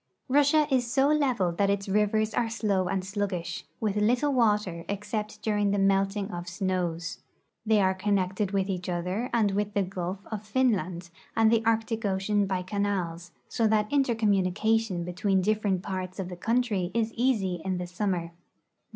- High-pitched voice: Yes, high, 200 Hz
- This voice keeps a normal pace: Yes, average, 170 wpm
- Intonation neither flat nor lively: Yes, average, 3.0 semitones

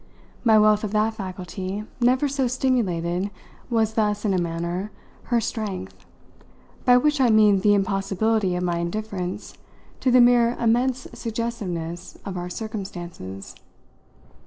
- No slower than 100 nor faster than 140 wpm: Yes, slow, 135 wpm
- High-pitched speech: Yes, high, 210 Hz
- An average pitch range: Yes, average, 4.5 semitones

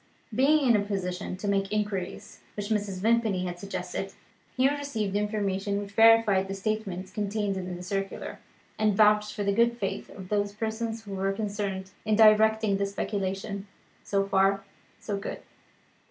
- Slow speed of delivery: No, average, 165 wpm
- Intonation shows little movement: Yes, narrow, 1.8 semitones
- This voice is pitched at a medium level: No, high, 205 Hz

